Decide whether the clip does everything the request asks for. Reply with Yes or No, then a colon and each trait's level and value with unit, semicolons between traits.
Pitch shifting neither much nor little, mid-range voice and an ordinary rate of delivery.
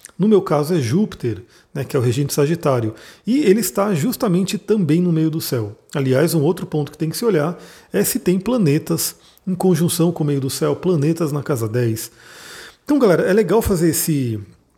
No: average, 4.8 semitones; medium, 160 Hz; fast, 205 wpm